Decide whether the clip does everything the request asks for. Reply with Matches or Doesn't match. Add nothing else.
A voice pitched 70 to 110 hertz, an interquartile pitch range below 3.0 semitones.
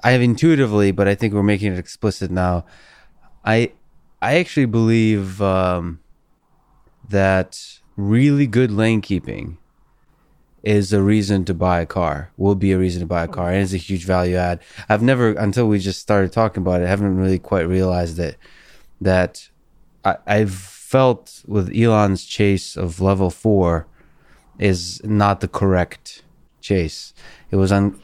Matches